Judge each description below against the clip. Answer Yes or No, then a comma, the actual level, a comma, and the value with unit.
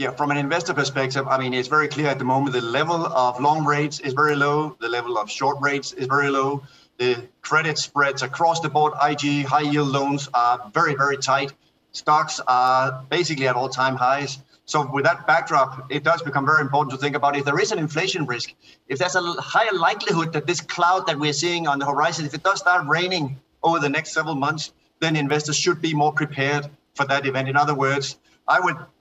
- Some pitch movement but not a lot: No, narrow, 2.1 semitones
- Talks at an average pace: No, fast, 220 wpm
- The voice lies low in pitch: No, medium, 145 Hz